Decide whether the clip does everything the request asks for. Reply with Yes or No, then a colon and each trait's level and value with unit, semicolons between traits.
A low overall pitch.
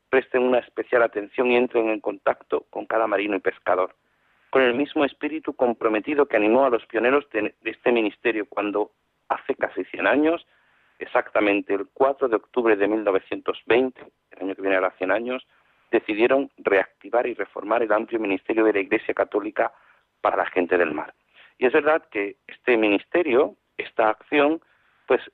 Yes: low, 115 Hz